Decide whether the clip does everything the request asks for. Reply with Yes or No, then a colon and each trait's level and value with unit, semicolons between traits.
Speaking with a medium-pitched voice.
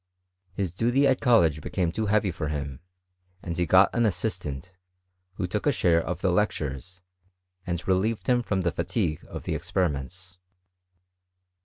No: very low, 90 Hz